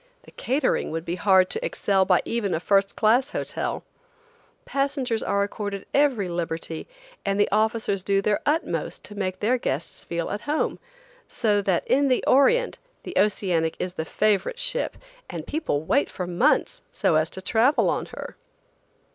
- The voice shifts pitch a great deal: Yes, wide, 5.8 semitones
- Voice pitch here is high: Yes, high, 205 Hz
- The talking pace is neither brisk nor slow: Yes, average, 165 wpm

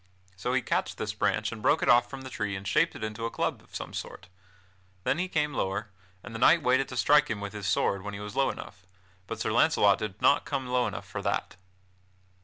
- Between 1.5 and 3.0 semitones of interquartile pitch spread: No, average, 4.5 semitones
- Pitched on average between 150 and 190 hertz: No, low, 110 Hz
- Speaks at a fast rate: Yes, fast, 240 wpm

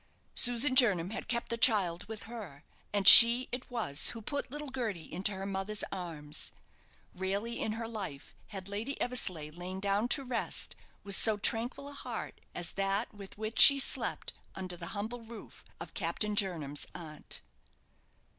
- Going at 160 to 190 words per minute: Yes, average, 165 wpm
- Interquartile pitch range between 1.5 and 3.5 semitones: No, average, 4.1 semitones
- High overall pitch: Yes, high, 210 Hz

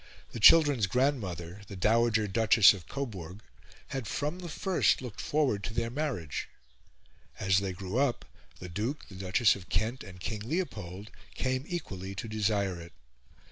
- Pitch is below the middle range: Yes, low, 110 Hz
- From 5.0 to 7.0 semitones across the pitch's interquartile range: Yes, average, 5.3 semitones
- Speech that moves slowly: No, average, 155 wpm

